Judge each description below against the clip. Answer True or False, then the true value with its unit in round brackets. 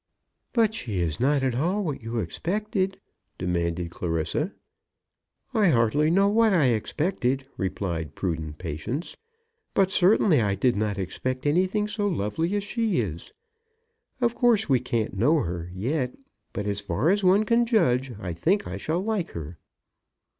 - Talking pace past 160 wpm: False (155 wpm)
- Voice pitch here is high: False (135 Hz)